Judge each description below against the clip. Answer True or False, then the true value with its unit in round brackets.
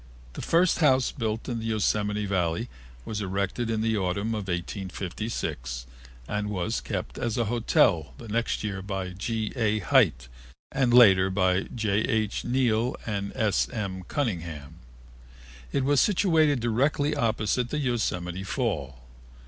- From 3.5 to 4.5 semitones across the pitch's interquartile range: True (4.1 semitones)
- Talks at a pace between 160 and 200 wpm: False (140 wpm)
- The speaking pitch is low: True (110 Hz)